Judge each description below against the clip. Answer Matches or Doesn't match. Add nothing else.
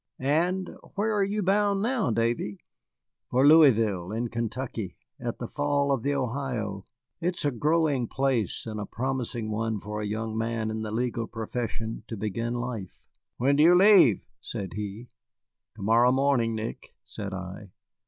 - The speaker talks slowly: Doesn't match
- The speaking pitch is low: Matches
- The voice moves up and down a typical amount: Matches